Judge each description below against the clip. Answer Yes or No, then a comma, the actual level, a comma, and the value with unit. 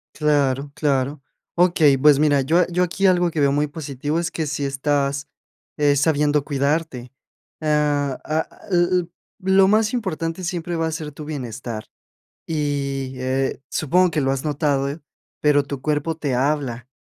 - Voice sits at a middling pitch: Yes, medium, 150 Hz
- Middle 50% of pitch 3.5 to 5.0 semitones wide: No, average, 2.9 semitones